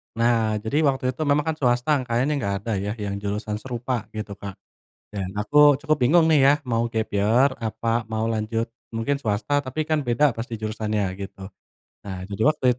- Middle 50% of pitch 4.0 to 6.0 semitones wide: Yes, average, 4.3 semitones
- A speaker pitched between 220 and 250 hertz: No, low, 115 Hz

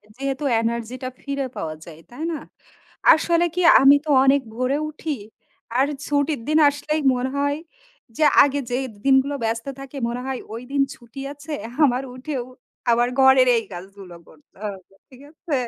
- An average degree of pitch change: Yes, average, 3.2 semitones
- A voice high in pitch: Yes, very high, 265 Hz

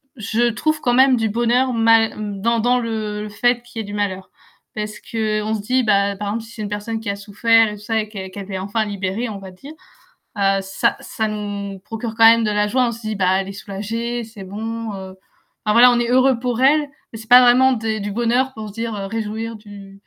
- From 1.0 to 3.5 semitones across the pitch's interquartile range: Yes, narrow, 2.5 semitones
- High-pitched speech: Yes, high, 220 Hz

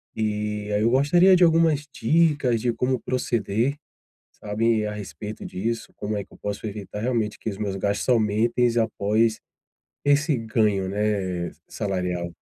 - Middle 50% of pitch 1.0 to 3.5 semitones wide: Yes, average, 3.2 semitones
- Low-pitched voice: Yes, low, 110 Hz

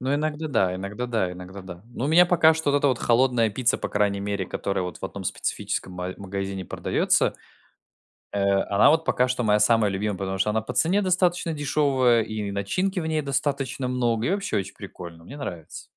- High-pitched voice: No, low, 115 Hz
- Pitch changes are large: Yes, wide, 6.5 semitones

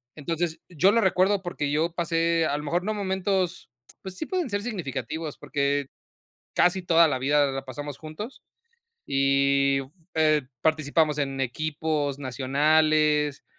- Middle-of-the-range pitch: Yes, medium, 155 Hz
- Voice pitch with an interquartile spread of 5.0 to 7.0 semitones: No, average, 3.7 semitones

